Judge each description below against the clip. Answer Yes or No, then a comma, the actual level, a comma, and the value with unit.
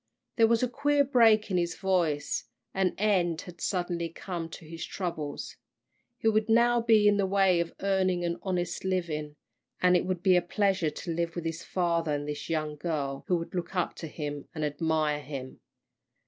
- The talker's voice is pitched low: No, medium, 175 Hz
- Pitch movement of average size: Yes, average, 3.3 semitones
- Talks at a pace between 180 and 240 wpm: Yes, average, 190 wpm